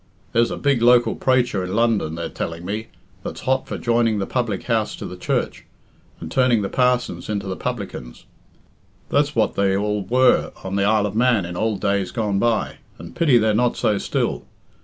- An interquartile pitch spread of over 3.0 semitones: Yes, average, 3.7 semitones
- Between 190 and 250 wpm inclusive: Yes, average, 195 wpm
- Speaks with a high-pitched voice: No, low, 110 Hz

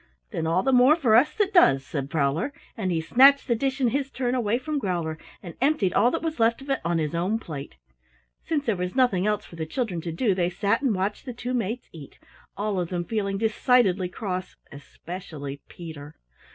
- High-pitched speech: Yes, high, 205 Hz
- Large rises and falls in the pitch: Yes, wide, 6.7 semitones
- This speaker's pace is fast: Yes, fast, 215 wpm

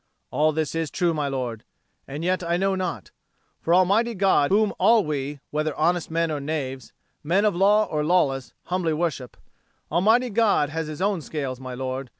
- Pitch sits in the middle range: Yes, medium, 160 Hz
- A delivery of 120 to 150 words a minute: No, average, 180 wpm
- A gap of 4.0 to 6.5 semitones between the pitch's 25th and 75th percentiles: Yes, average, 4.6 semitones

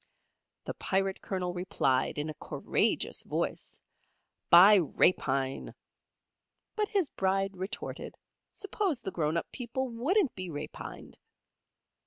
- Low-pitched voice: No, high, 190 Hz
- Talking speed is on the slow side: Yes, slow, 110 wpm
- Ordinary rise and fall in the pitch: No, wide, 6.5 semitones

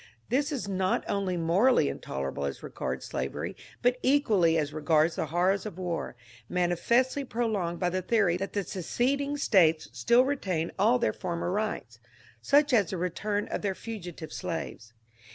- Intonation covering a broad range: Yes, wide, 5.8 semitones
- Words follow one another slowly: No, average, 165 wpm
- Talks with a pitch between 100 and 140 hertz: No, medium, 185 Hz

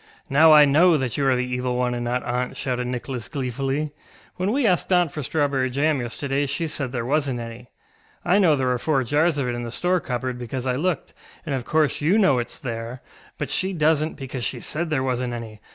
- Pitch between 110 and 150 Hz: Yes, low, 135 Hz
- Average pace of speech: No, fast, 225 wpm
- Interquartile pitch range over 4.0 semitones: No, average, 3.7 semitones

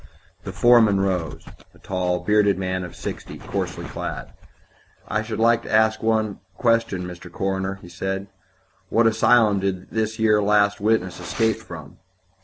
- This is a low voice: Yes, low, 100 Hz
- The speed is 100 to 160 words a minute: Yes, average, 150 wpm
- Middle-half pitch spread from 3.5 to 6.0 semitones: No, average, 3.1 semitones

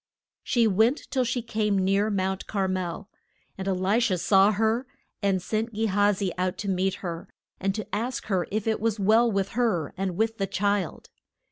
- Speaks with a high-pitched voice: Yes, high, 200 Hz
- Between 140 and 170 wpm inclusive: No, average, 200 wpm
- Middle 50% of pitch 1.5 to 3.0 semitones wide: Yes, average, 2.7 semitones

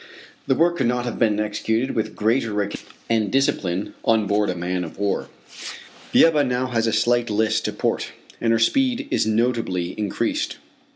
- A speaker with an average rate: Yes, average, 180 wpm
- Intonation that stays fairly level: No, average, 3.0 semitones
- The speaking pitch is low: Yes, low, 110 Hz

